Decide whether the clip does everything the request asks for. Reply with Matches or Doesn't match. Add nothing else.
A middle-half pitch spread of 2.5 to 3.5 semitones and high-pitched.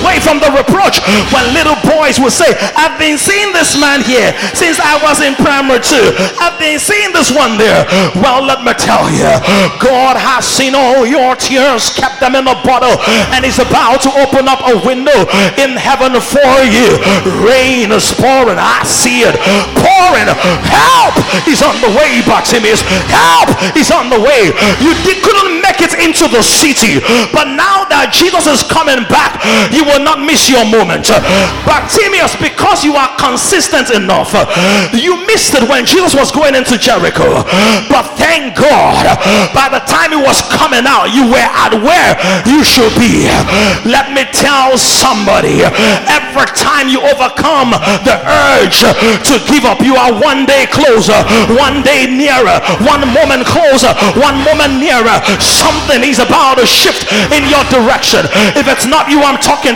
Matches